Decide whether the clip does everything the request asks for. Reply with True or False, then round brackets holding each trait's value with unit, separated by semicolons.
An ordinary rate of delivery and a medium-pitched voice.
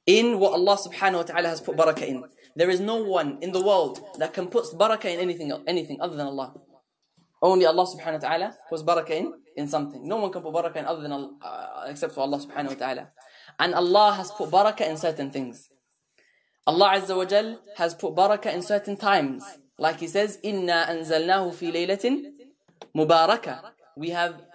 True (195 wpm; 175 Hz)